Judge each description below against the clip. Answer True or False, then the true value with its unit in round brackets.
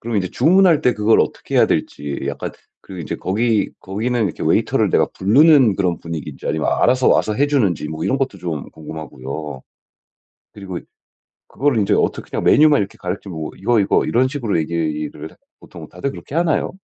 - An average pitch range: False (7.6 semitones)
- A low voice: True (100 Hz)